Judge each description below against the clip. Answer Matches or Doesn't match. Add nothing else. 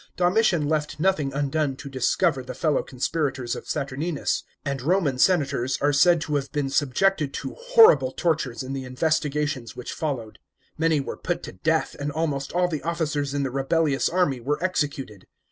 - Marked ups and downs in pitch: Doesn't match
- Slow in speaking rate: Doesn't match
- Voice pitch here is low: Doesn't match